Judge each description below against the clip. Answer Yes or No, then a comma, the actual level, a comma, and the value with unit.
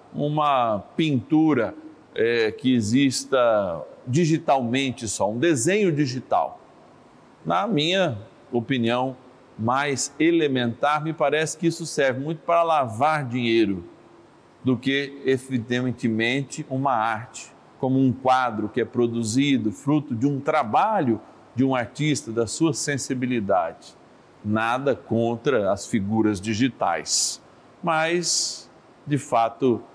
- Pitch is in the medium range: No, low, 130 Hz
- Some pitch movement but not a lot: Yes, average, 4.2 semitones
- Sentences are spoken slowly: Yes, slow, 105 wpm